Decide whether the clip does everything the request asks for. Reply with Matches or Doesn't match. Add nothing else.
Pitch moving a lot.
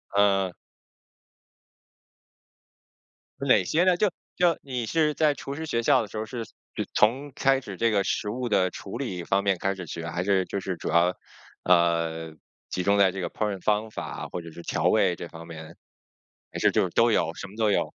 Doesn't match